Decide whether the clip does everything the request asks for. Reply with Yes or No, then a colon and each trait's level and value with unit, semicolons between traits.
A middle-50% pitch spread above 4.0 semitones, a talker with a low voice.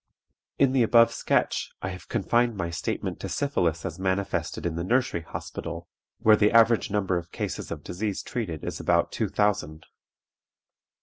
Yes: average, 5.2 semitones; low, 100 Hz